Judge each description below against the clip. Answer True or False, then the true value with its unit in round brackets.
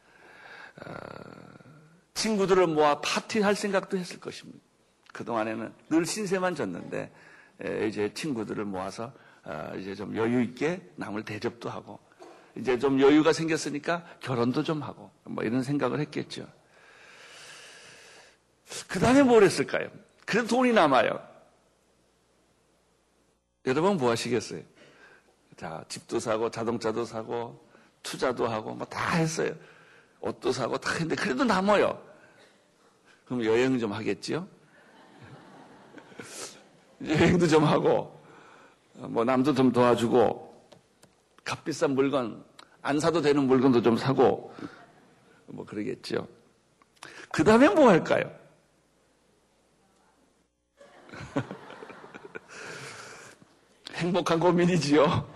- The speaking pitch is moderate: True (145 Hz)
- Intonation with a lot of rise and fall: True (6.6 semitones)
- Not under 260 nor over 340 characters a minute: False (215 characters per minute)